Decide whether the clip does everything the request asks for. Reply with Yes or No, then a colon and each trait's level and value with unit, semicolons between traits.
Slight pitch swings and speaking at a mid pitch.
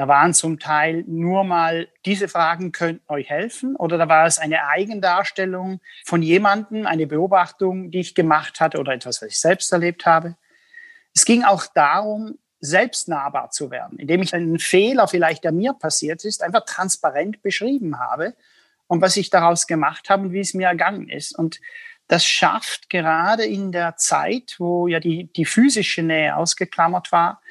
No: average, 3.5 semitones; medium, 180 Hz